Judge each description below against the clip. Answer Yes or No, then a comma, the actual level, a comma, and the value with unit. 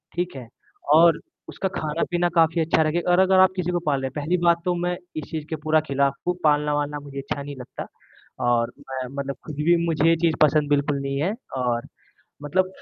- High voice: No, medium, 155 Hz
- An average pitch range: Yes, average, 3.6 semitones